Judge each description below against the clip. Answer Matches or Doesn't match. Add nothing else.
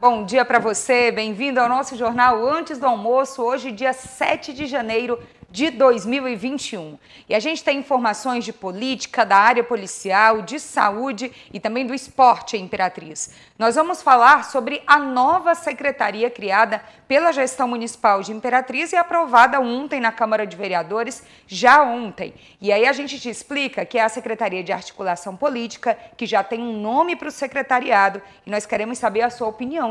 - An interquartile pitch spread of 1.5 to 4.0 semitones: Matches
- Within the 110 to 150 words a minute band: Doesn't match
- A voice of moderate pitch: Doesn't match